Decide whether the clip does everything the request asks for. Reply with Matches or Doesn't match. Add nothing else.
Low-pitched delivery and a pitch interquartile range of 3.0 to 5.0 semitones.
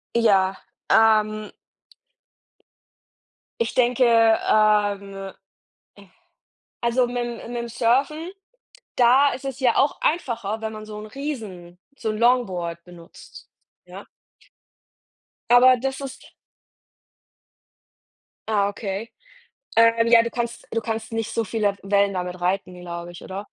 Doesn't match